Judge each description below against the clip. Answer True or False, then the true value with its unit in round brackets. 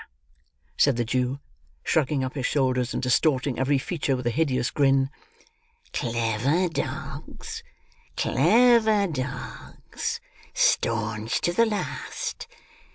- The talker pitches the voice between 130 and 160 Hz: True (135 Hz)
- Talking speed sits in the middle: False (105 wpm)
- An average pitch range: True (4.0 semitones)